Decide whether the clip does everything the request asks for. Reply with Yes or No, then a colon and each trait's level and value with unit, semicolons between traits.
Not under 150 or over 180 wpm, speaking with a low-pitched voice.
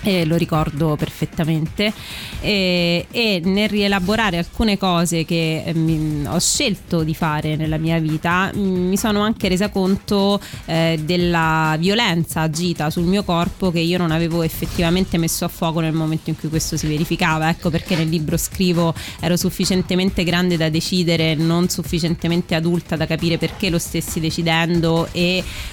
No: average, 155 wpm; medium, 170 Hz